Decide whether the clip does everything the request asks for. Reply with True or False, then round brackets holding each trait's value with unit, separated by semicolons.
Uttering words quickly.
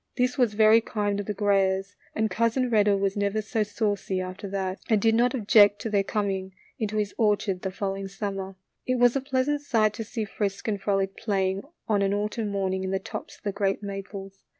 True (210 wpm)